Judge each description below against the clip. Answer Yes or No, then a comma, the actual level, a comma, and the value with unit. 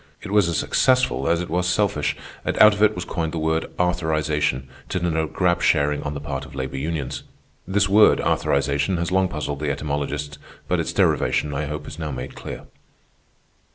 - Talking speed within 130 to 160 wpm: No, average, 190 wpm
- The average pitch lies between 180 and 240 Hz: No, very low, 80 Hz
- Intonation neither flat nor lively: Yes, average, 3.6 semitones